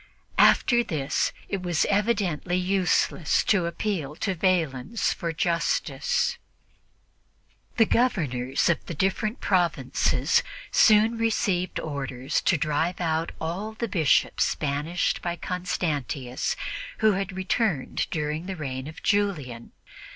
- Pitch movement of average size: Yes, average, 4.9 semitones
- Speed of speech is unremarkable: No, slow, 115 wpm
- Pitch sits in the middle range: Yes, medium, 175 Hz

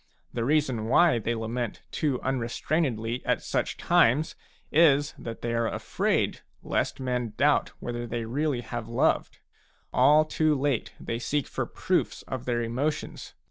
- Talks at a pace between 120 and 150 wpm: Yes, average, 145 wpm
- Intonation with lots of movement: No, average, 3.9 semitones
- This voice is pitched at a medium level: No, low, 125 Hz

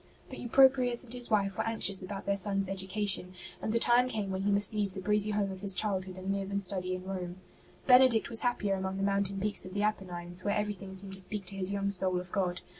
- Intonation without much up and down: Yes, narrow, 1.9 semitones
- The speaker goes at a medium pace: No, fast, 245 wpm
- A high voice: Yes, high, 195 Hz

